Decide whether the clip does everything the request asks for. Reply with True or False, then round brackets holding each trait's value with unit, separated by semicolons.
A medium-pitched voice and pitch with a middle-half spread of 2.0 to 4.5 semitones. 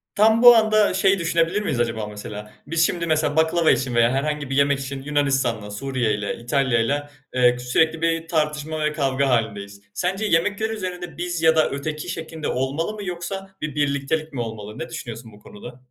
False (150 Hz; 5.3 semitones)